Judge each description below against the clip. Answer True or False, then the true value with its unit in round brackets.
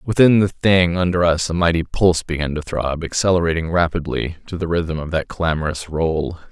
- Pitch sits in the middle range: False (85 Hz)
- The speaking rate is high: False (185 wpm)